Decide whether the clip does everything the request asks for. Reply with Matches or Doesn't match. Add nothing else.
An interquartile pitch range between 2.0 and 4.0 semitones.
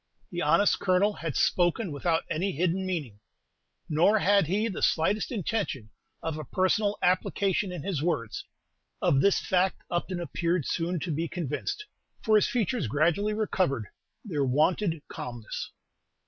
Doesn't match